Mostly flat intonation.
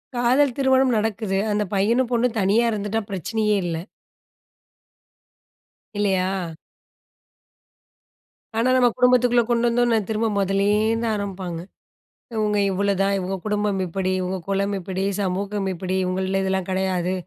No: average, 3.3 semitones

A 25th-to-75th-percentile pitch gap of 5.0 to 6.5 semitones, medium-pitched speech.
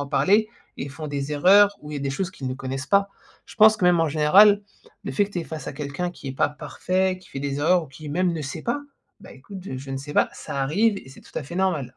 Yes: average, 5.3 semitones; medium, 155 Hz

